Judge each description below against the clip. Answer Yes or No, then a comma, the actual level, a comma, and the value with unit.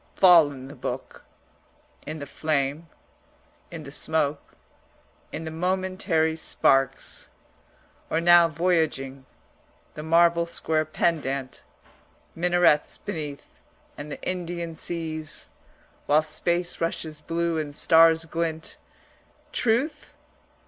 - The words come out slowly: Yes, slow, 100 wpm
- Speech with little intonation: Yes, narrow, 2.3 semitones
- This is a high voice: No, medium, 160 Hz